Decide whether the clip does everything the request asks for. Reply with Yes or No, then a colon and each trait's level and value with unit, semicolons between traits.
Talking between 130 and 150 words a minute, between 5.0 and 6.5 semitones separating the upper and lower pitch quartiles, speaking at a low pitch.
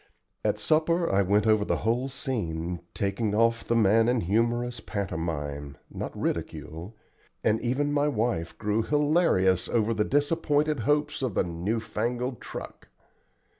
Yes: average, 140 wpm; average, 5.3 semitones; low, 115 Hz